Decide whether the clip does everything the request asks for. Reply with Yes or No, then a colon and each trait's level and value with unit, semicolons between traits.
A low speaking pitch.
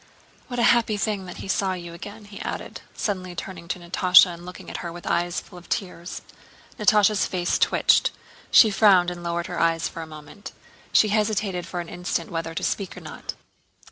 No: medium, 180 Hz